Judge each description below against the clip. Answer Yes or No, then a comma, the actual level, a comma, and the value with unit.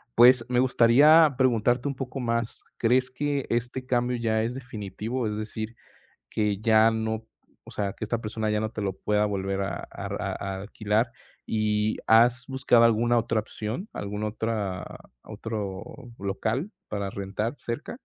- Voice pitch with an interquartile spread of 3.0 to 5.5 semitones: No, narrow, 2.6 semitones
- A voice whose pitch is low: Yes, low, 115 Hz